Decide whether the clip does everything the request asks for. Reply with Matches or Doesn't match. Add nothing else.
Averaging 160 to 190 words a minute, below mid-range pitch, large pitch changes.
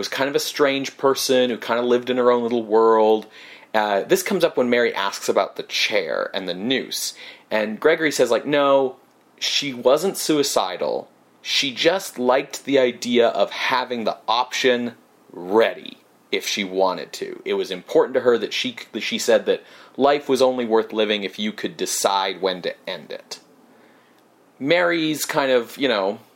Matches